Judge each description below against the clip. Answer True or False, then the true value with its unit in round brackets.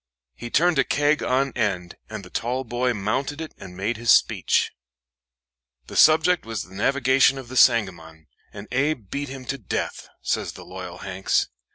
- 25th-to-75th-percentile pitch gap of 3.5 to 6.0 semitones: True (5.3 semitones)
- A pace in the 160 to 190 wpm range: True (175 wpm)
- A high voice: False (125 Hz)